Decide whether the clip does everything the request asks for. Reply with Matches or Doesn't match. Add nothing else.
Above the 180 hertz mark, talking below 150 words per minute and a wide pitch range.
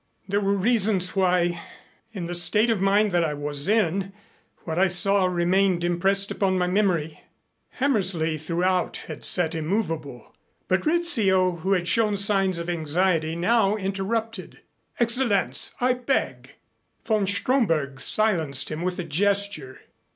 Doesn't match